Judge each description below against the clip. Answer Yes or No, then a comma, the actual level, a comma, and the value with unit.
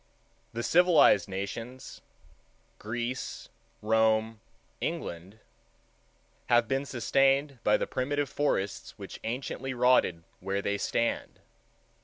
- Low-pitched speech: Yes, low, 115 Hz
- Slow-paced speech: Yes, slow, 85 wpm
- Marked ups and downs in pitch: No, average, 4.4 semitones